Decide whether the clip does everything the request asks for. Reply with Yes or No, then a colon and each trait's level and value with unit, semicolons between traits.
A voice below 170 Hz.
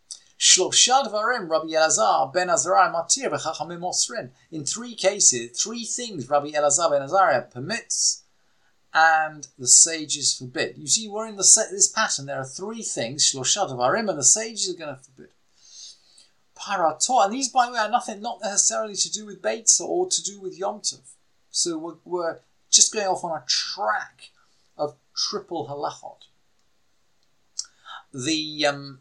No: medium, 180 Hz